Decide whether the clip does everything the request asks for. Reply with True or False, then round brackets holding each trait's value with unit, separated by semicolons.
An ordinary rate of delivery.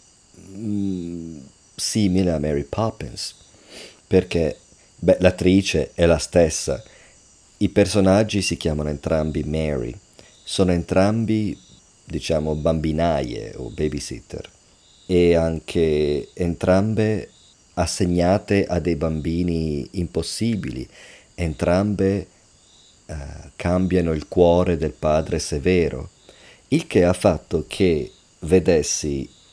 False (90 wpm)